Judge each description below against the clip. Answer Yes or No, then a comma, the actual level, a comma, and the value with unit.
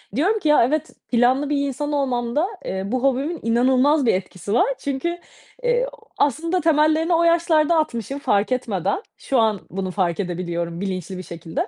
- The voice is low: No, very high, 265 Hz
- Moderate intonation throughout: No, wide, 7.5 semitones